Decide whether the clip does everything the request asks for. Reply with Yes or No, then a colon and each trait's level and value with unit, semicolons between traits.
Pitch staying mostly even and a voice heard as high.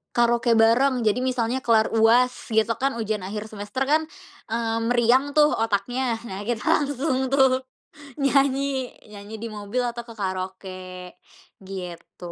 No: average, 3.5 semitones; high, 230 Hz